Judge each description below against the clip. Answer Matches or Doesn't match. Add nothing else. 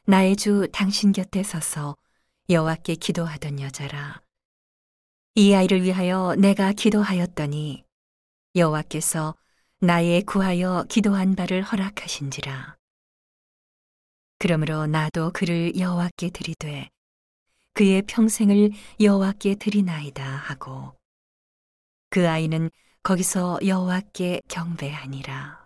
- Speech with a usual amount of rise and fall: Matches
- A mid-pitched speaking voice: Matches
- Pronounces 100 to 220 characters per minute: Doesn't match